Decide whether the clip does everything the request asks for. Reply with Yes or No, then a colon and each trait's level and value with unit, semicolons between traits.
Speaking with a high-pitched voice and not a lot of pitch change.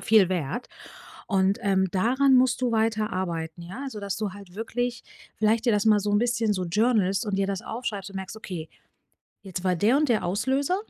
No: high, 210 Hz; average, 3.7 semitones